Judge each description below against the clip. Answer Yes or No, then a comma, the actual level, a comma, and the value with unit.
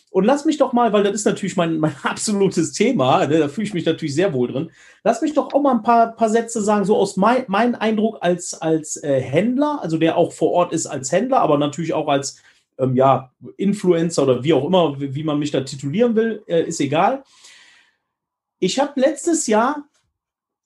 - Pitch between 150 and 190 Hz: Yes, medium, 185 Hz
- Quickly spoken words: Yes, fast, 215 wpm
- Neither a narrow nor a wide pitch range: No, wide, 7.0 semitones